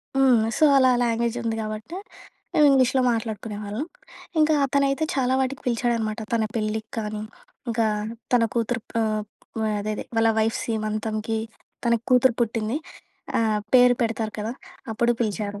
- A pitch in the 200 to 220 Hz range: No, high, 230 Hz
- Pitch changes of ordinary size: No, narrow, 2.3 semitones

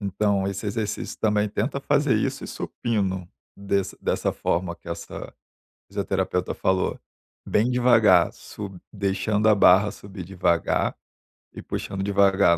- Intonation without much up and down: Yes, narrow, 2.1 semitones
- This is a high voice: No, low, 100 Hz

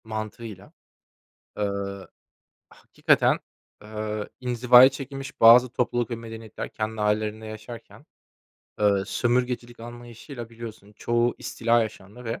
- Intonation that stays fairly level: Yes, narrow, 1.9 semitones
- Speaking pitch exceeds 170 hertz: No, low, 115 Hz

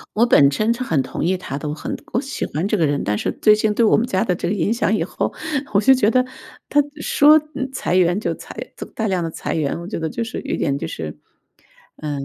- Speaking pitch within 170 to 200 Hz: Yes, high, 190 Hz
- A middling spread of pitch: No, wide, 6.2 semitones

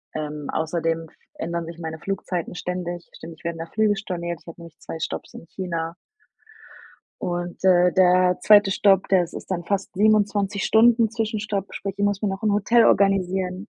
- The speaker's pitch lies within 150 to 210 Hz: Yes, medium, 185 Hz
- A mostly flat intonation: No, average, 3.1 semitones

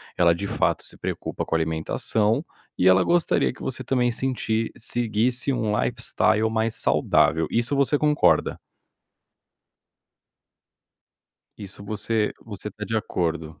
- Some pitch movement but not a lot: Yes, average, 4.2 semitones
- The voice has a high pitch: No, low, 110 Hz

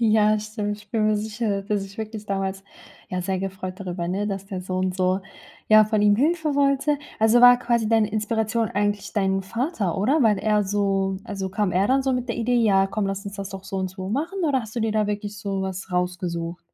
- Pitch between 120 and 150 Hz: No, high, 205 Hz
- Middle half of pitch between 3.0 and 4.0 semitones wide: No, narrow, 2.5 semitones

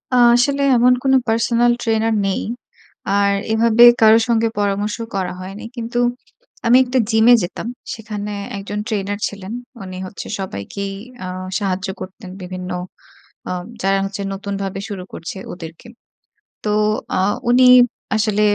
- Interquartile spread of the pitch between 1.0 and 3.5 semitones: Yes, average, 2.8 semitones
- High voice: Yes, high, 205 Hz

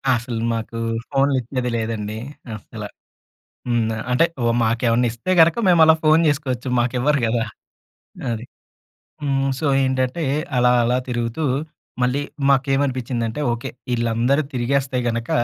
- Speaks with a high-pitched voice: No, low, 125 Hz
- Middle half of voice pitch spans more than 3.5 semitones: No, average, 2.9 semitones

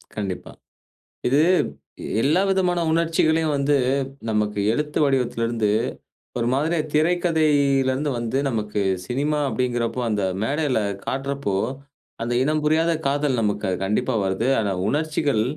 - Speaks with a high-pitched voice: No, low, 135 Hz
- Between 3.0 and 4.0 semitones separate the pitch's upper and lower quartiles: No, average, 4.9 semitones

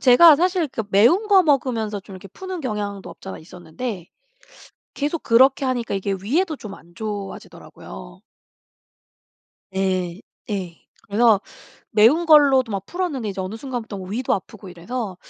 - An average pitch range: No, wide, 6.0 semitones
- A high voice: Yes, high, 220 Hz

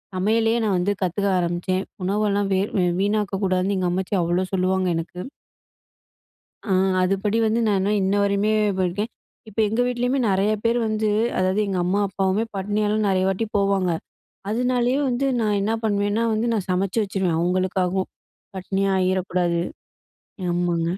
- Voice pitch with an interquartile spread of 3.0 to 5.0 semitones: No, narrow, 2.4 semitones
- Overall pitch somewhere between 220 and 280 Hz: No, high, 195 Hz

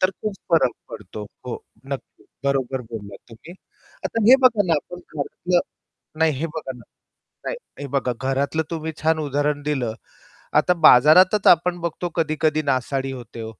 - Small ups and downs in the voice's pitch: No, average, 4.2 semitones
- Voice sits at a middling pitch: Yes, medium, 150 Hz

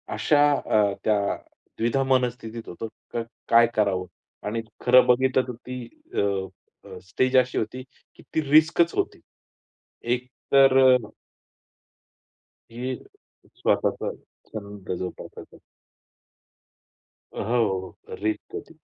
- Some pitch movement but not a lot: Yes, average, 3.7 semitones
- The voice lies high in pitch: No, low, 120 Hz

